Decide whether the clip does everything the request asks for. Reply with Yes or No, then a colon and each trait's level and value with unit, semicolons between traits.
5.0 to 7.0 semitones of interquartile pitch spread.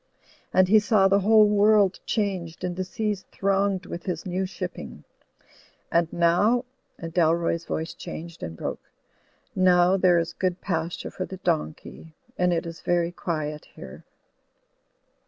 No: narrow, 2.6 semitones